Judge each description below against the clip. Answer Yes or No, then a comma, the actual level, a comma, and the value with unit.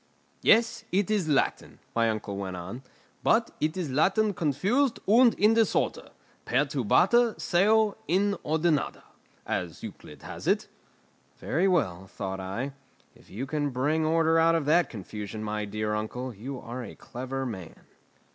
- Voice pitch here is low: No, medium, 145 Hz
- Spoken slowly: No, average, 145 wpm